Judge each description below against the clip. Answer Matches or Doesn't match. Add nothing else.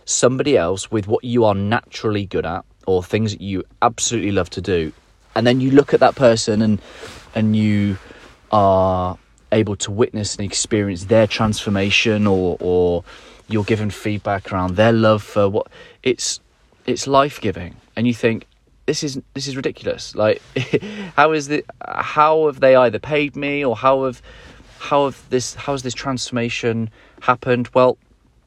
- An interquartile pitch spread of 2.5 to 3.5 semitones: Doesn't match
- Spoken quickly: Doesn't match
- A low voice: Matches